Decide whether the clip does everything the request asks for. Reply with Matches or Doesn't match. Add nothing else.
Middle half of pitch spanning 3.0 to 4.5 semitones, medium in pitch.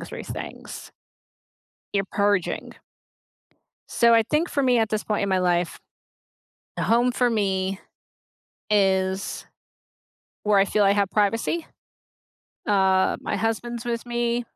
Doesn't match